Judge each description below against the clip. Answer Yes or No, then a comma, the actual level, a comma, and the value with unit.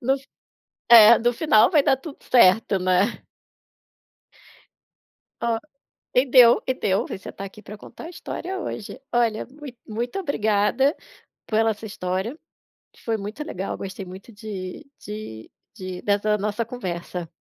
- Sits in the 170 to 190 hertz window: No, high, 220 Hz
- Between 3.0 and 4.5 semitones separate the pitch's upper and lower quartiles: Yes, average, 4.0 semitones